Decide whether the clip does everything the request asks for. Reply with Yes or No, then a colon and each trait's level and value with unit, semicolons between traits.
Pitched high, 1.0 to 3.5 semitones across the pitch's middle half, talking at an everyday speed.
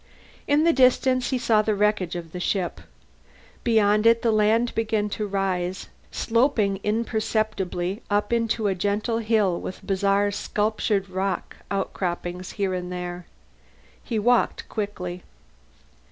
No: high, 205 Hz; average, 3.2 semitones; slow, 130 wpm